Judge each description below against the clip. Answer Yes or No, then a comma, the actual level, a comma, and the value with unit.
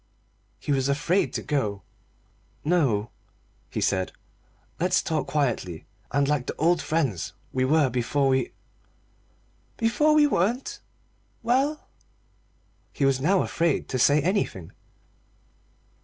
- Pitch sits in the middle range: Yes, medium, 145 Hz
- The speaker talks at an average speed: No, slow, 120 wpm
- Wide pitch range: Yes, wide, 5.7 semitones